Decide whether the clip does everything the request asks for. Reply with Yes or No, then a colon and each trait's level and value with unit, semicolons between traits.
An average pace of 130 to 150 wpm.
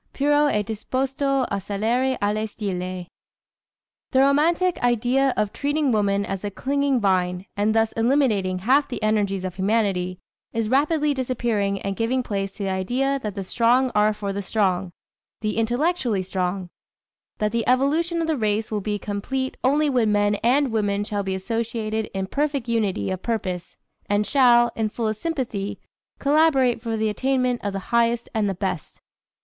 No: average, 165 wpm